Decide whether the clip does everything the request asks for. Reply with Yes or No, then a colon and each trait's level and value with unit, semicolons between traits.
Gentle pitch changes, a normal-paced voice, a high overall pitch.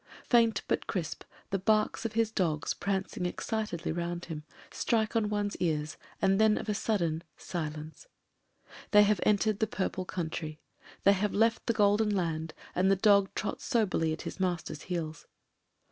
No: average, 4.1 semitones; average, 170 wpm; high, 195 Hz